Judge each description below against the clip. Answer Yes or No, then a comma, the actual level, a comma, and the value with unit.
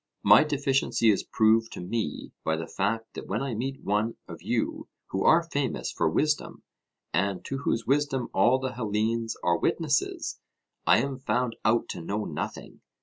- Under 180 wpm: Yes, average, 170 wpm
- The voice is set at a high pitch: No, low, 115 Hz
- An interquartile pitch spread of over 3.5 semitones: Yes, average, 4.6 semitones